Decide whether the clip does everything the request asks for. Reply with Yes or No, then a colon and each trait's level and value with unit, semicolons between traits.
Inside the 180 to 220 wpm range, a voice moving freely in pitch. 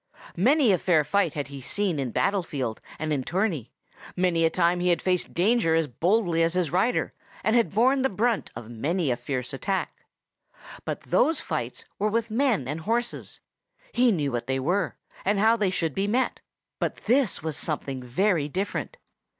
Yes: average, 185 wpm; wide, 6.4 semitones